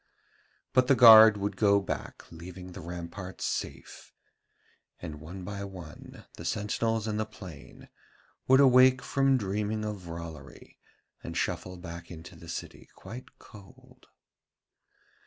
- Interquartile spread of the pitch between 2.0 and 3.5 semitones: No, average, 3.9 semitones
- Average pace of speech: No, slow, 130 wpm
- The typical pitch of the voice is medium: No, low, 100 Hz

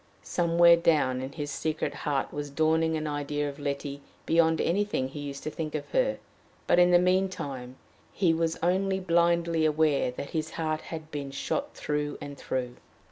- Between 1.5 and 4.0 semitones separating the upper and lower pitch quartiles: Yes, average, 2.9 semitones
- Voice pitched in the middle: Yes, medium, 155 Hz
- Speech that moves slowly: No, average, 180 wpm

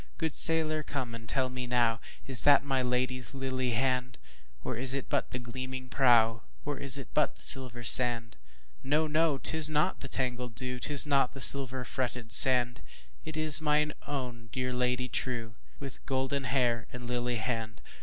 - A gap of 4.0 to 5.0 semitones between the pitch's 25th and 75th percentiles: No, narrow, 2.5 semitones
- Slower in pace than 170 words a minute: Yes, average, 155 wpm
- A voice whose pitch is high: No, low, 125 Hz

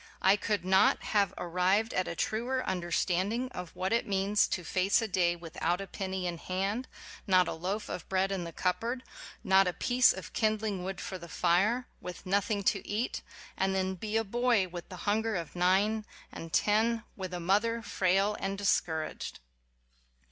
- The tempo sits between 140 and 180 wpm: No, average, 190 wpm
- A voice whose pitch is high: Yes, high, 195 Hz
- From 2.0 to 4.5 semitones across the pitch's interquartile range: Yes, average, 3.0 semitones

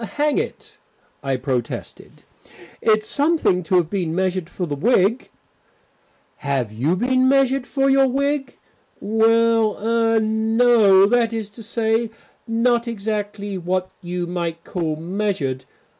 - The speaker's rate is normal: No, slow, 130 wpm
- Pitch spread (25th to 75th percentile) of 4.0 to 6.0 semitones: Yes, average, 4.7 semitones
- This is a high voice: Yes, high, 215 Hz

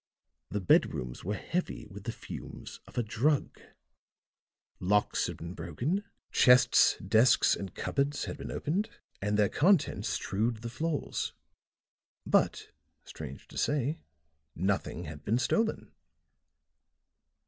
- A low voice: Yes, low, 115 Hz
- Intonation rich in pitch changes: Yes, wide, 6.8 semitones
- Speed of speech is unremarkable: No, slow, 120 wpm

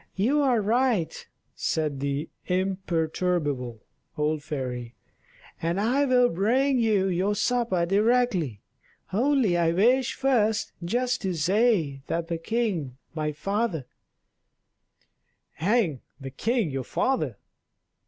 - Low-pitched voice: No, high, 190 Hz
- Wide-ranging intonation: Yes, wide, 7.4 semitones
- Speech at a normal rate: No, slow, 115 wpm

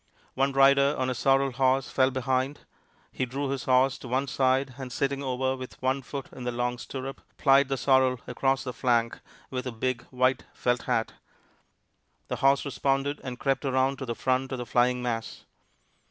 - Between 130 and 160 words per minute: No, average, 185 wpm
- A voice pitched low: Yes, low, 130 Hz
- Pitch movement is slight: Yes, narrow, 1.3 semitones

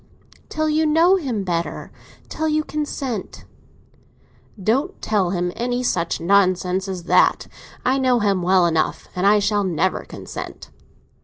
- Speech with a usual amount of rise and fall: No, wide, 6.8 semitones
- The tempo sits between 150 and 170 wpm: No, slow, 135 wpm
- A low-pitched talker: No, high, 205 Hz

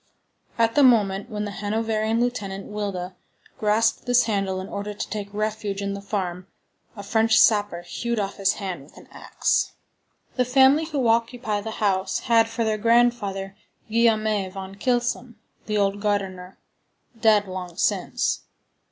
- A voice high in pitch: Yes, high, 210 Hz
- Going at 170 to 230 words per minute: No, average, 150 wpm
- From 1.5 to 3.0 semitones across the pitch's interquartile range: Yes, narrow, 2.6 semitones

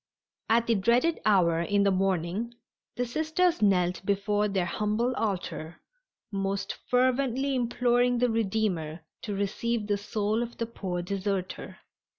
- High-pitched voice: Yes, high, 210 Hz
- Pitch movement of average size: Yes, average, 3.7 semitones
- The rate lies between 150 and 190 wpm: No, slow, 135 wpm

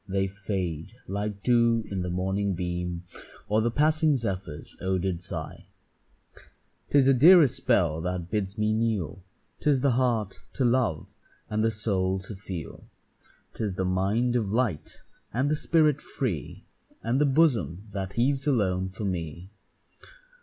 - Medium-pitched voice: No, low, 105 Hz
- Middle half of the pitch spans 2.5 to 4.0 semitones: No, average, 4.9 semitones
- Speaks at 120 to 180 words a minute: Yes, average, 145 wpm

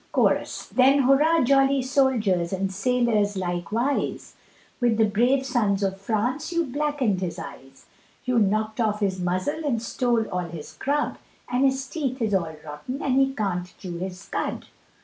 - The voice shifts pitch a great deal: Yes, wide, 5.9 semitones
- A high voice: Yes, high, 225 Hz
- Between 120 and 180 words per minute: Yes, average, 160 wpm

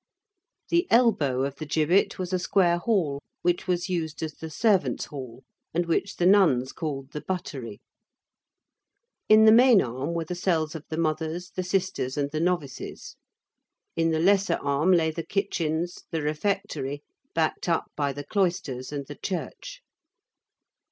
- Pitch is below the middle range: No, medium, 165 Hz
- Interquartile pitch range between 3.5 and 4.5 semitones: Yes, average, 4.1 semitones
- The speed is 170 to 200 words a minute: No, average, 160 wpm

